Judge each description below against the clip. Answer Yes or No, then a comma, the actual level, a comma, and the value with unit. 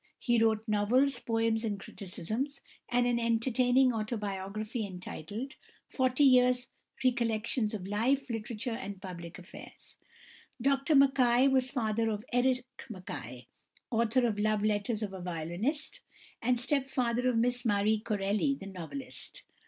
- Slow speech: Yes, slow, 130 wpm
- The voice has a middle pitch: No, high, 230 Hz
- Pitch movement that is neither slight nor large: Yes, average, 3.5 semitones